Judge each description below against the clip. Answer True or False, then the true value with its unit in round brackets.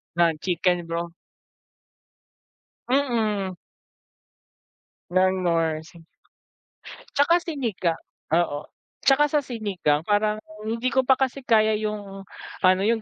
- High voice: True (205 Hz)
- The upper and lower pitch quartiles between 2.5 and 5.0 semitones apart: False (5.6 semitones)